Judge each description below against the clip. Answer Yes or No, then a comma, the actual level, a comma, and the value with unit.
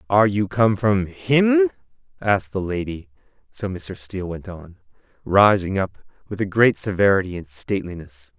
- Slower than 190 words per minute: Yes, average, 150 wpm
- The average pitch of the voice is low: Yes, very low, 95 Hz